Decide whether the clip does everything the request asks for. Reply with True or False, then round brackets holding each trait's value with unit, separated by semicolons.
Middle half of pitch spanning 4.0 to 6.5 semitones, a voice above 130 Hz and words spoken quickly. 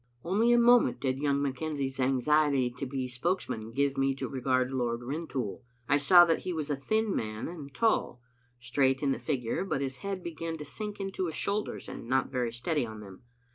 True (4.7 semitones; 140 Hz; 210 wpm)